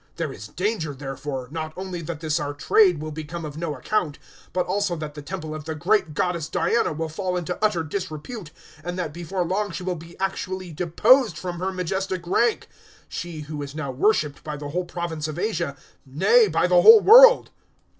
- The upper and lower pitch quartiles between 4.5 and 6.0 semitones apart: No, average, 3.6 semitones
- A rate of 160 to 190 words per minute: No, average, 200 wpm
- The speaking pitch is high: No, medium, 170 Hz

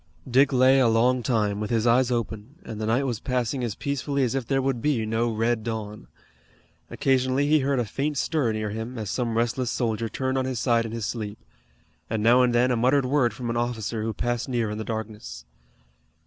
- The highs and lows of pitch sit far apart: No, average, 2.7 semitones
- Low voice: Yes, low, 120 Hz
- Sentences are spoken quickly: Yes, fast, 220 wpm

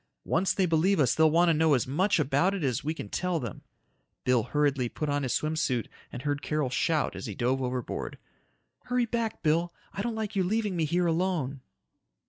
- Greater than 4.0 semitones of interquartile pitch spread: Yes, average, 5.2 semitones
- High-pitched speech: No, medium, 155 Hz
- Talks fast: Yes, fast, 210 wpm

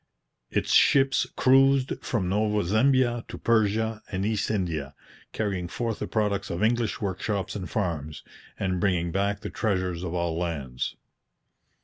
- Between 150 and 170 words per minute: No, average, 140 wpm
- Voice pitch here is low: Yes, low, 100 Hz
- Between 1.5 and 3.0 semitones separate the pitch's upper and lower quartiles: No, average, 4.0 semitones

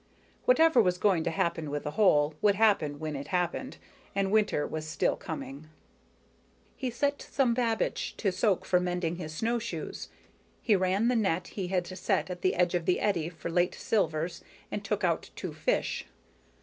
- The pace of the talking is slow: No, average, 175 wpm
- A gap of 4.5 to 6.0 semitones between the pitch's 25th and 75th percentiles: Yes, average, 4.8 semitones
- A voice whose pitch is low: No, medium, 180 Hz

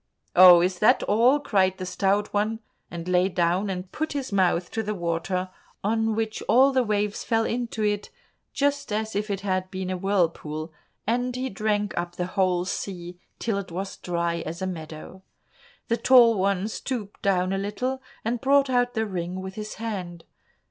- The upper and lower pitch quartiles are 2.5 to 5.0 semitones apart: Yes, average, 3.7 semitones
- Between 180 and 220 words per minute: Yes, average, 185 wpm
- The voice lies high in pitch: Yes, high, 200 Hz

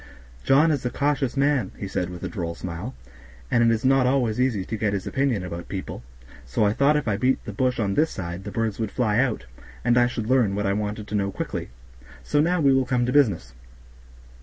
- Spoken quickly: Yes, fast, 235 wpm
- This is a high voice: No, low, 115 Hz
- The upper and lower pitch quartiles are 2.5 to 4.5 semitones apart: No, average, 5.0 semitones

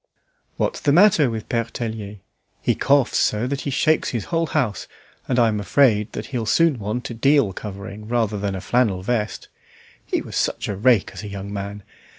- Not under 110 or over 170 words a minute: No, average, 185 wpm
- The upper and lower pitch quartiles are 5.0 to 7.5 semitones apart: No, average, 4.1 semitones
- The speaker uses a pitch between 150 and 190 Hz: No, low, 110 Hz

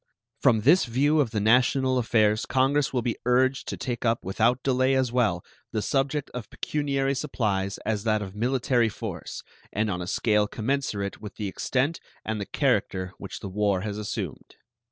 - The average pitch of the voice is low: Yes, low, 115 Hz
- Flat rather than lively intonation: No, average, 4.0 semitones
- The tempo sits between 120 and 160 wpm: No, average, 175 wpm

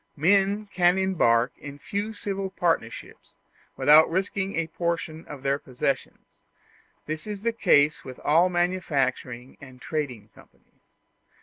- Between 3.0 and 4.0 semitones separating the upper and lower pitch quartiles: No, wide, 5.6 semitones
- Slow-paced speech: Yes, slow, 125 wpm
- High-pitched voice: No, medium, 165 Hz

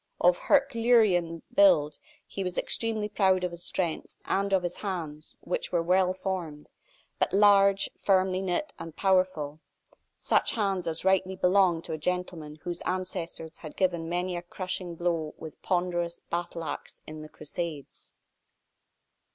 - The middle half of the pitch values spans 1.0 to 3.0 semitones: Yes, narrow, 2.5 semitones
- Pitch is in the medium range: Yes, medium, 180 Hz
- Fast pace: No, average, 145 wpm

